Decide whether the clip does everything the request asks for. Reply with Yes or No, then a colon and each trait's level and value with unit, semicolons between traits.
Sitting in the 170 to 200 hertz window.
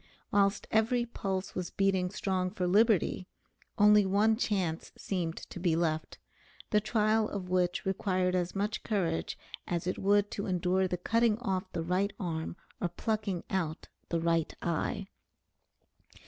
Yes: high, 190 Hz